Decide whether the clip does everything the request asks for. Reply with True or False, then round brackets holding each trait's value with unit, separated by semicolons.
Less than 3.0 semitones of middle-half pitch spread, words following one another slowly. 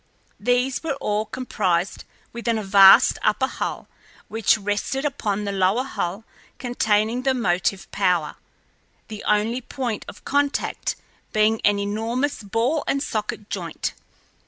False (3.7 semitones; 130 wpm)